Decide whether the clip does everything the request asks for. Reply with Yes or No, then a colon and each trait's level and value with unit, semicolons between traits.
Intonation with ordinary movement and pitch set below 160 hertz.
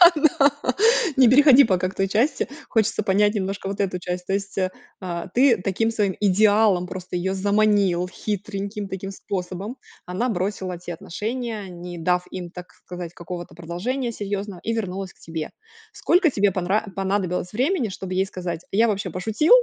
No: average, 3.0 semitones; high, 195 Hz